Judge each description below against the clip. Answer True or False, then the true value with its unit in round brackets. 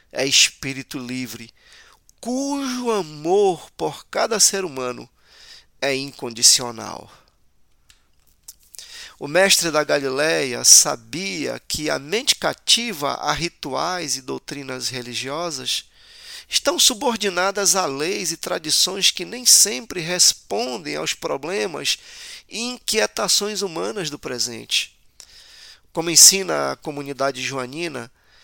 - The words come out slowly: True (100 wpm)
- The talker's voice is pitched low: False (175 Hz)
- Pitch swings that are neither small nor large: False (8.3 semitones)